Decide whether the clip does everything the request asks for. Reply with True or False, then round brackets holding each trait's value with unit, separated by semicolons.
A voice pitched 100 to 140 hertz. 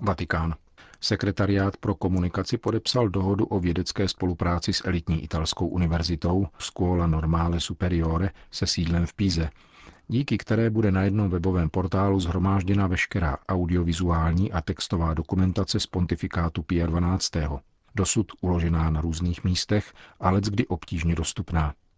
False (90 Hz)